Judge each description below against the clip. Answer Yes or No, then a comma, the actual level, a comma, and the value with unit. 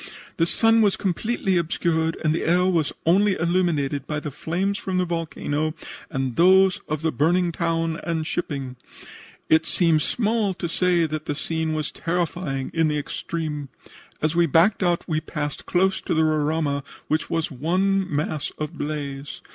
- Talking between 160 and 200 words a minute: Yes, average, 165 wpm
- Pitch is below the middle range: No, medium, 165 Hz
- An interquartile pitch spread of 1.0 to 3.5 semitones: Yes, average, 2.8 semitones